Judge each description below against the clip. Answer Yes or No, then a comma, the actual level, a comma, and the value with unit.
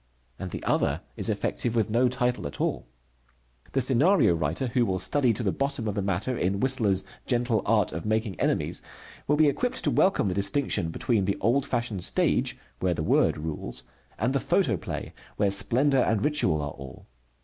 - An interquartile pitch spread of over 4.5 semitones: Yes, wide, 5.4 semitones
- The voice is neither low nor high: No, low, 110 Hz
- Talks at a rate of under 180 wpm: No, average, 185 wpm